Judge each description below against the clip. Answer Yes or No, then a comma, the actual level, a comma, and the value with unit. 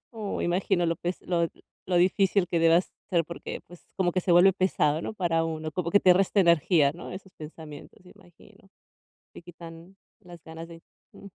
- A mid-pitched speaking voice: Yes, medium, 175 Hz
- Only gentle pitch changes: Yes, narrow, 2.2 semitones